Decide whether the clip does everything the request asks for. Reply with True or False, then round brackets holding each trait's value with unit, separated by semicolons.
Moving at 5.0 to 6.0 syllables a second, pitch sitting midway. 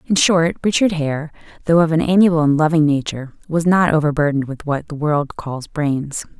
True (5.4 syllables/s; 155 Hz)